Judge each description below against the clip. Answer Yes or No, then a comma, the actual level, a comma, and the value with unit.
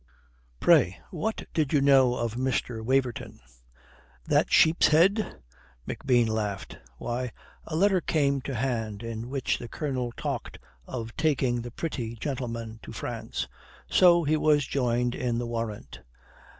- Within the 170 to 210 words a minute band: No, slow, 135 wpm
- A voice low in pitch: Yes, low, 125 Hz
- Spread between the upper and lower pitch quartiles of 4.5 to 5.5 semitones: No, average, 4.1 semitones